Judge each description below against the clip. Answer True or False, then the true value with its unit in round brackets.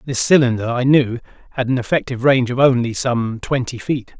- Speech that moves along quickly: False (185 wpm)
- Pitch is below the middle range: True (125 Hz)